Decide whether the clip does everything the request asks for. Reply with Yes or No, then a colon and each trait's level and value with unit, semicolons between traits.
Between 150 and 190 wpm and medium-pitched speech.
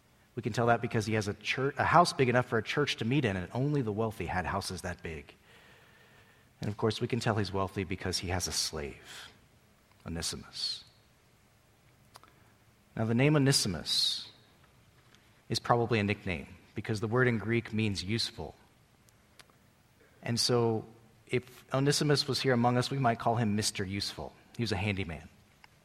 No: average, 170 wpm; low, 115 Hz